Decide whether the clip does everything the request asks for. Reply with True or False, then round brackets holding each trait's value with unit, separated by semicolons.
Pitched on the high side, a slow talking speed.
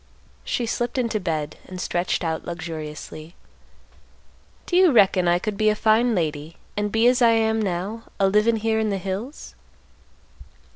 False (205 Hz; 160 wpm)